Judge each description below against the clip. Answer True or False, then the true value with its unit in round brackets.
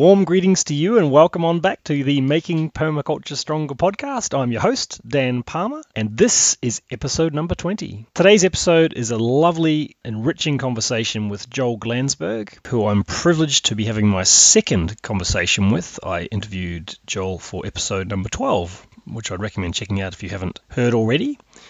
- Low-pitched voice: True (125 Hz)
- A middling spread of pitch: False (7.4 semitones)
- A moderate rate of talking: True (170 wpm)